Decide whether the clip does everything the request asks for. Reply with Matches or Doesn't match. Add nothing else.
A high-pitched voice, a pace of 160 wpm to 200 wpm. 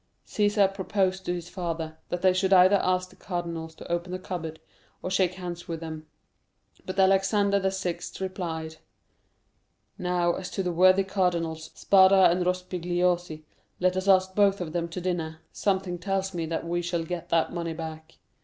Doesn't match